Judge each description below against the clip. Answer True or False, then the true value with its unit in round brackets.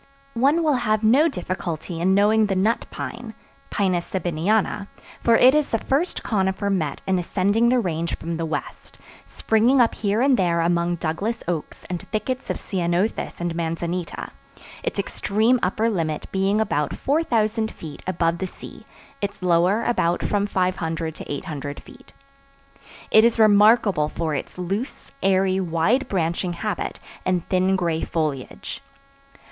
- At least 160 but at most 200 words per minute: False (150 wpm)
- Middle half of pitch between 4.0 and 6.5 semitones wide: True (4.5 semitones)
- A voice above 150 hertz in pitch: True (190 Hz)